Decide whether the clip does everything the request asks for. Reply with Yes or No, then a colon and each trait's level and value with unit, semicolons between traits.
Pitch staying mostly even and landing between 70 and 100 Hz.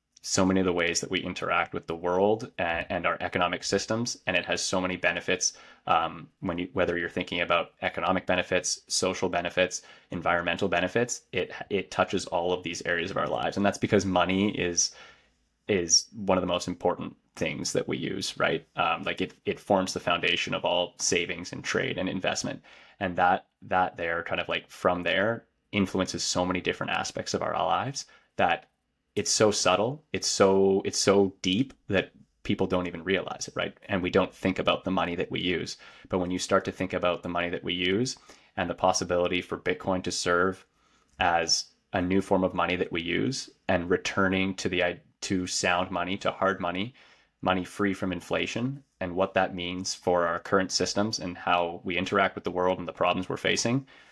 Yes: narrow, 1.6 semitones; very low, 90 Hz